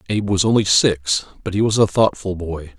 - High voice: No, very low, 95 Hz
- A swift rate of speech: Yes, fast, 215 wpm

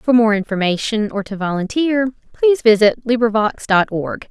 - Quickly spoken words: No, average, 155 wpm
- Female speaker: Yes, female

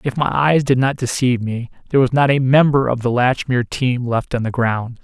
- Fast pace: Yes, fast, 240 wpm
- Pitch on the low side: Yes, low, 125 Hz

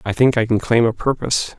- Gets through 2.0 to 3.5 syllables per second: No, 6.0 syllables/s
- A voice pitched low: Yes, low, 115 Hz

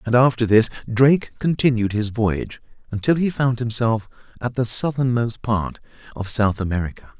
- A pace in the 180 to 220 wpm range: No, average, 150 wpm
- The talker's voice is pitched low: Yes, low, 120 Hz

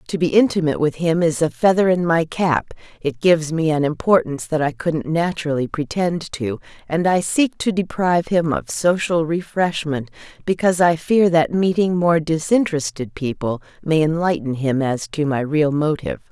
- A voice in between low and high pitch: Yes, medium, 160 Hz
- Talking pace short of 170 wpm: No, average, 175 wpm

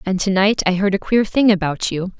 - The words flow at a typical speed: No, fast, 275 wpm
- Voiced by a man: No, female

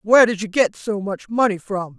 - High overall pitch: Yes, high, 205 Hz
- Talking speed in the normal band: No, fast, 240 wpm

